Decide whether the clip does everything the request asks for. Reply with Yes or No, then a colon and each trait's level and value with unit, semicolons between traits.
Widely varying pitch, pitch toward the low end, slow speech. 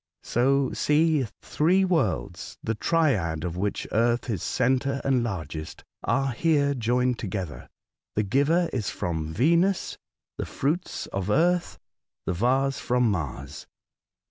Yes: wide, 6.6 semitones; low, 125 Hz; slow, 125 wpm